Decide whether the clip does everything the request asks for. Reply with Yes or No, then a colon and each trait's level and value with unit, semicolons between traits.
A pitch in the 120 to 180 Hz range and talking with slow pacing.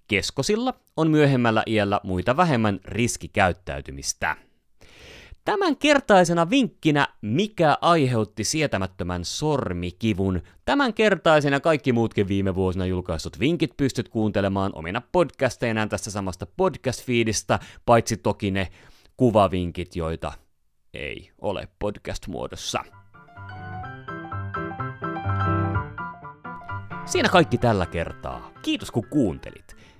No: low, 110 Hz; slow, 90 wpm